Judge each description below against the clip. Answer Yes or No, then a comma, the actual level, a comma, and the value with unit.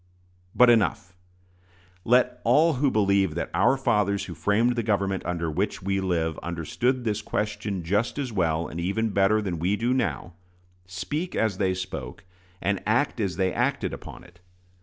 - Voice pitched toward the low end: Yes, low, 100 Hz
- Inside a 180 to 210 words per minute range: No, average, 165 wpm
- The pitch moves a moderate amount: Yes, average, 3.9 semitones